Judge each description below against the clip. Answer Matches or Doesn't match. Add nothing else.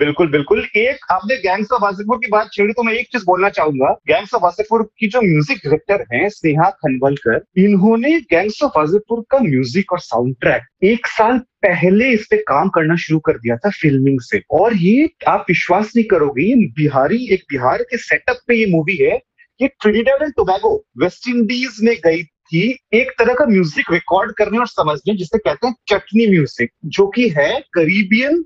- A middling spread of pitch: Doesn't match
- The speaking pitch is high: Matches